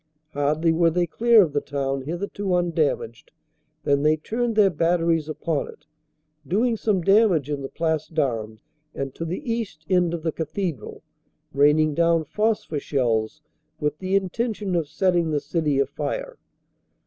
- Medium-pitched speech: Yes, medium, 165 Hz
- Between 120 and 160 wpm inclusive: Yes, average, 155 wpm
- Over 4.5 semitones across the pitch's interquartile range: Yes, average, 4.9 semitones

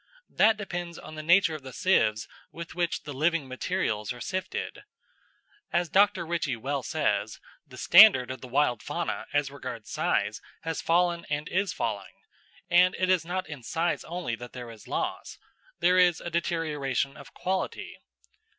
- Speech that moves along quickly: No, average, 165 wpm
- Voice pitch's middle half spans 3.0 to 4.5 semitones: No, wide, 5.4 semitones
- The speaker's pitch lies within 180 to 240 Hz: No, medium, 160 Hz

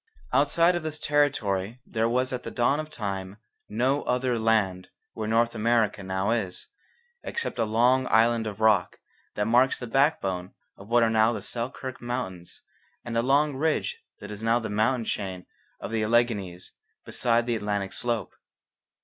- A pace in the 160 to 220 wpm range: Yes, average, 165 wpm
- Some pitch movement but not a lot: Yes, average, 3.4 semitones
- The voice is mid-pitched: No, low, 115 Hz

